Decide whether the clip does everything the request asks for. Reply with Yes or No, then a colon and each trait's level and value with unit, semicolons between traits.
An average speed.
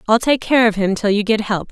No: fast, 315 wpm